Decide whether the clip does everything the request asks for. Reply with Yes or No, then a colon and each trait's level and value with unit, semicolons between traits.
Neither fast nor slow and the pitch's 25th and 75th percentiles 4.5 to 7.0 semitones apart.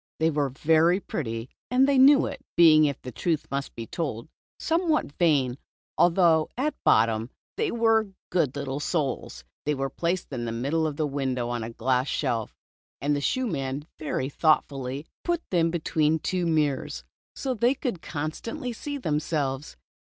Yes: average, 165 wpm; average, 5.0 semitones